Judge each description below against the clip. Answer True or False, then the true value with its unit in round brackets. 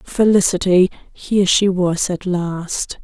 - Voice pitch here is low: False (185 Hz)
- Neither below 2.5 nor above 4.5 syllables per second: True (3.7 syllables/s)